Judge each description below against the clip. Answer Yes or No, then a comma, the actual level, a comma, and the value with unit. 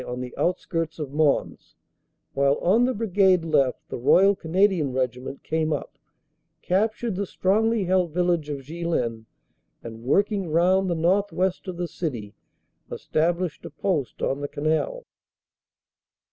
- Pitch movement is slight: No, average, 4.9 semitones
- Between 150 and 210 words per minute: No, average, 140 wpm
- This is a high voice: No, medium, 170 Hz